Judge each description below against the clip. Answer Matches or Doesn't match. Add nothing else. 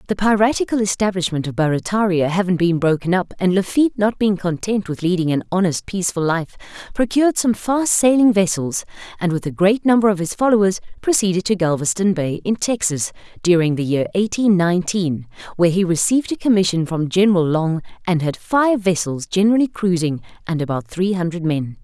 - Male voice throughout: Doesn't match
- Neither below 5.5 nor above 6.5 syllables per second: Matches